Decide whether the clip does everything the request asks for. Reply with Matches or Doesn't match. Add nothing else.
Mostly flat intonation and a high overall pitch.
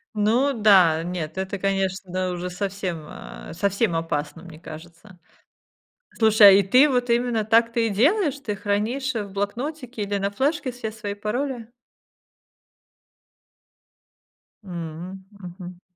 Doesn't match